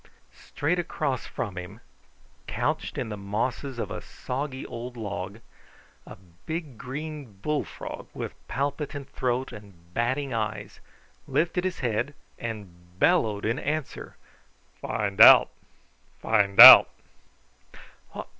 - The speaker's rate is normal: No, slow, 110 wpm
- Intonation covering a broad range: Yes, wide, 5.7 semitones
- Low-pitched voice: Yes, low, 120 Hz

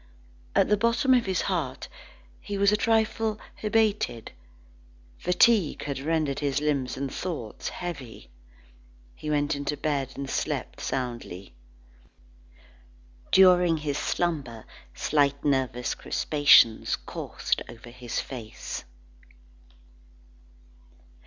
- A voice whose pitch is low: No, medium, 145 Hz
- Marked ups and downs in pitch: Yes, wide, 6.0 semitones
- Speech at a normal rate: No, slow, 105 wpm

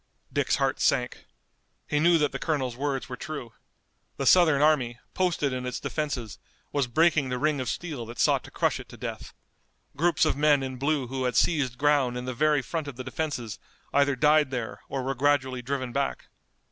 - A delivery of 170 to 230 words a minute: Yes, average, 195 wpm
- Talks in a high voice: No, medium, 140 Hz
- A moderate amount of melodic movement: Yes, average, 3.0 semitones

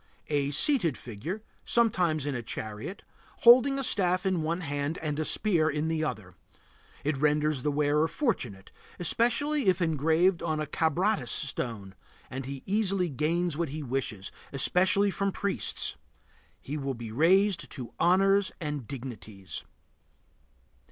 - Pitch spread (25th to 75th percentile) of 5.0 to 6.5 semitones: Yes, average, 5.3 semitones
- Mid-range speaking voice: Yes, medium, 155 Hz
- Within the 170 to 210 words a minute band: No, average, 140 wpm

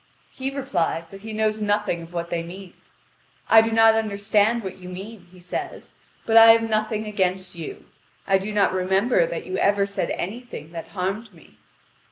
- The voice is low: No, high, 200 Hz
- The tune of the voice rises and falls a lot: No, average, 3.4 semitones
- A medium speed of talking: Yes, average, 185 wpm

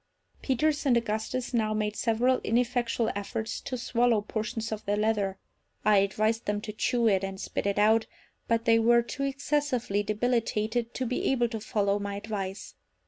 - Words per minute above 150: Yes, average, 170 wpm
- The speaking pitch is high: Yes, high, 225 Hz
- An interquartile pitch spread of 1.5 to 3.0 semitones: Yes, narrow, 2.5 semitones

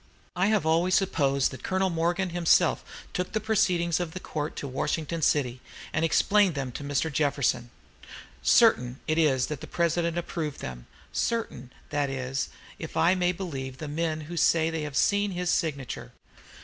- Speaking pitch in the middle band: Yes, medium, 160 Hz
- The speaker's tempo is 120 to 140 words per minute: No, average, 170 wpm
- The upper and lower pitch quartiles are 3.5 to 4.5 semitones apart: Yes, average, 4.1 semitones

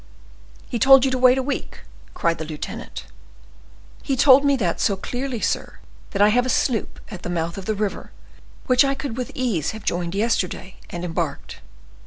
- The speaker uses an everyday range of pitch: No, wide, 6.4 semitones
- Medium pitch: No, high, 220 Hz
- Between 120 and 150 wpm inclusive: No, average, 190 wpm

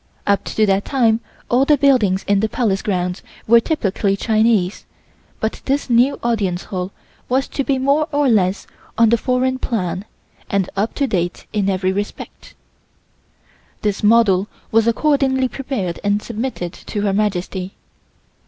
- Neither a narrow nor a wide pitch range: Yes, average, 4.8 semitones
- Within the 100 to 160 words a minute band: Yes, average, 150 wpm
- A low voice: No, high, 215 Hz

